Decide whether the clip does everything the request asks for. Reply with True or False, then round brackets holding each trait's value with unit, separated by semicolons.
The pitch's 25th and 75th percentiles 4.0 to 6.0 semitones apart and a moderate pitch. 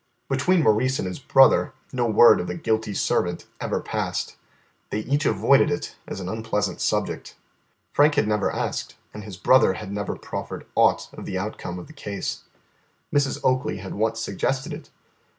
False (5.1 semitones; 110 Hz)